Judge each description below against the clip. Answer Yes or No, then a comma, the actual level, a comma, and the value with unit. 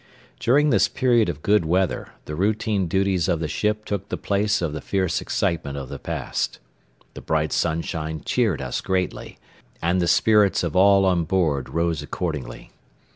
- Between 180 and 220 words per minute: No, average, 170 wpm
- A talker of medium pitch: No, very low, 90 Hz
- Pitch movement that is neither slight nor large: Yes, average, 4.1 semitones